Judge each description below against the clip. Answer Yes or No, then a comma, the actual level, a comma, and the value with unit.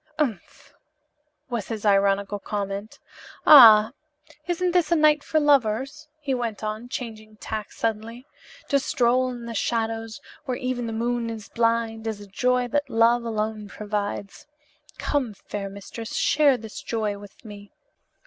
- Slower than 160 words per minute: Yes, average, 145 wpm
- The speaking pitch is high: Yes, high, 230 Hz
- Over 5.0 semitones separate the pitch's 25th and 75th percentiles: No, average, 3.1 semitones